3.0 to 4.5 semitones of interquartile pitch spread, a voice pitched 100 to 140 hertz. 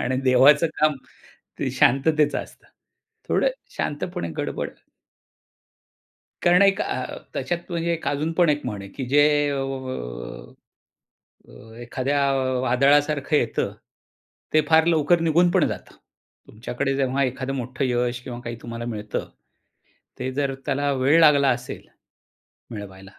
Yes: average, 3.7 semitones; low, 135 Hz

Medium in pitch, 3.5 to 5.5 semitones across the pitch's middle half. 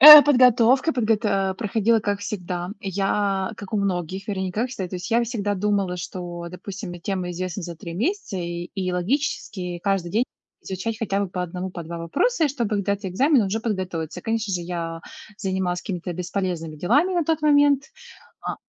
No: high, 195 Hz; average, 4.1 semitones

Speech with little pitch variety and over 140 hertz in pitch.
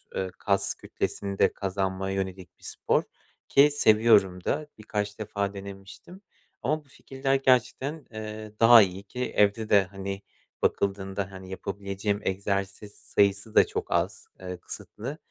No: narrow, 2.2 semitones; low, 100 Hz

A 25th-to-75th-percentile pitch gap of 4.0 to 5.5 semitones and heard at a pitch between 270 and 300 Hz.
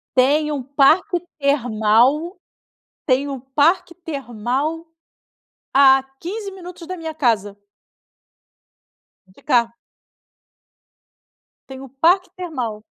Yes: average, 4.9 semitones; very high, 280 Hz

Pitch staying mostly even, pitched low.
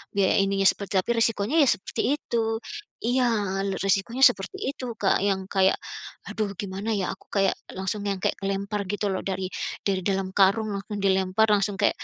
No: narrow, 2.1 semitones; high, 200 Hz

